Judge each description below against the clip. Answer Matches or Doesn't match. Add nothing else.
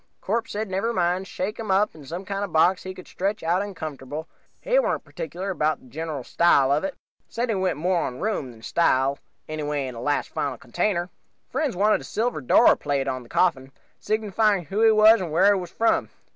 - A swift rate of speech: Matches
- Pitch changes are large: Matches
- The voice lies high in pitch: Doesn't match